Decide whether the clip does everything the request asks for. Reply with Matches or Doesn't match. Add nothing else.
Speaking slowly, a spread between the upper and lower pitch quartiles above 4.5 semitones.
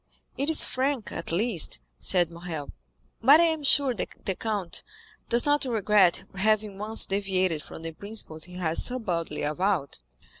Doesn't match